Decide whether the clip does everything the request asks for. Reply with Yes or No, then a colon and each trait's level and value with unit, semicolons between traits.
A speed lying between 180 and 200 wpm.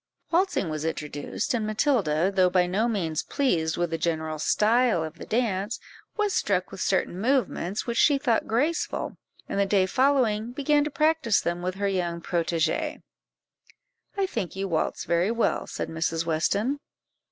No: average, 165 wpm